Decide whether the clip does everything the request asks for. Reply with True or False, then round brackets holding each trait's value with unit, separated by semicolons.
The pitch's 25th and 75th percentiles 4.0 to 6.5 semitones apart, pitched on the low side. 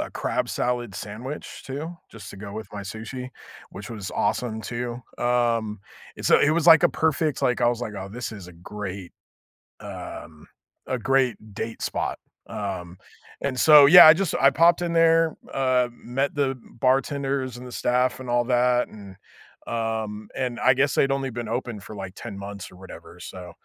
True (4.5 semitones; 120 Hz)